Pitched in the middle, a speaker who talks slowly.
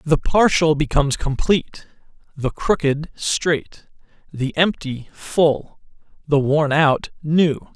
Yes: medium, 155 Hz; slow, 110 wpm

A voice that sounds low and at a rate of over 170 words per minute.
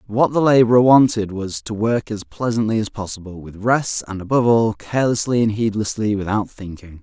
Yes: low, 110 Hz; average, 180 wpm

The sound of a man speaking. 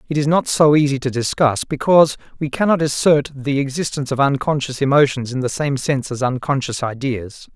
Yes: male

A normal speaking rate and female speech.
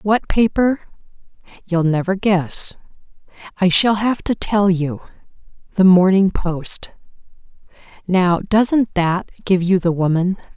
No: slow, 115 wpm; female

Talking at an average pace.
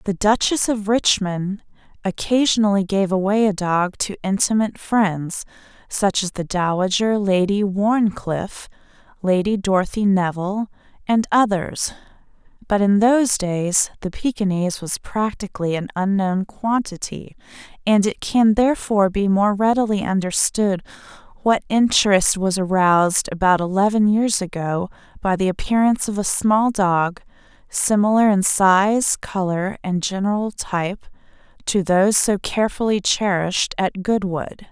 No: slow, 125 wpm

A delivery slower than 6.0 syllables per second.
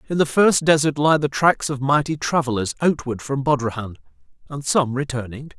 Yes: 5.3 syllables/s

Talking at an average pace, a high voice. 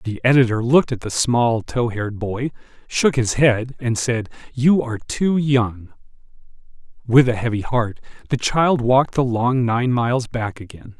No: average, 170 wpm; low, 120 Hz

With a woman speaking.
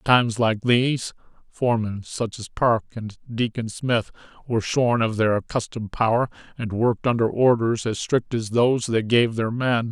No: male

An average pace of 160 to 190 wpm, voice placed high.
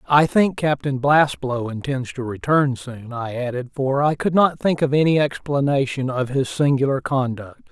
No: average, 170 wpm; low, 135 Hz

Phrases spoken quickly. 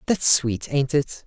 No: average, 190 wpm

